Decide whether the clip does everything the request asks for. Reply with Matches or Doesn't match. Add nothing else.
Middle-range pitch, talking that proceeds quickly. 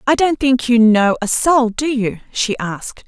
Doesn't match